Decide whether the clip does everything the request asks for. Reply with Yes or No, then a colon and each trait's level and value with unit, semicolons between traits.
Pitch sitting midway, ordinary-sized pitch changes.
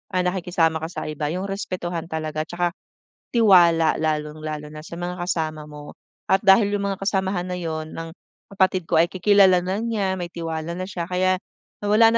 Yes: medium, 175 Hz; average, 3.1 semitones